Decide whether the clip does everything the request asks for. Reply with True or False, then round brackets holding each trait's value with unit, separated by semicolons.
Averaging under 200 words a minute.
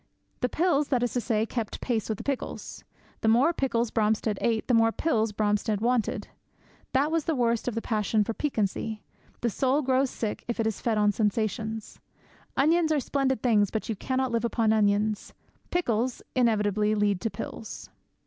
True (175 wpm)